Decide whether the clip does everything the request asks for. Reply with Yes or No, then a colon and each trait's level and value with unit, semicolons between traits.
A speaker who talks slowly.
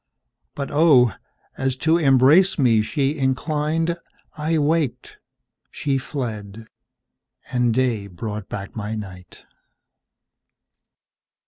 Yes: slow, 90 wpm